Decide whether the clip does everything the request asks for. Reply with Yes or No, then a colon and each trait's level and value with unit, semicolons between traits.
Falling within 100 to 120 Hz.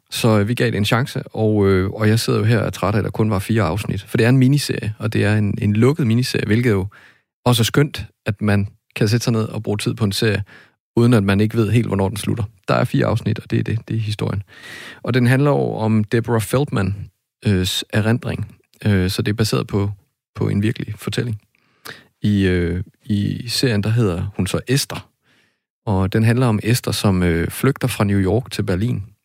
Yes: low, 110 Hz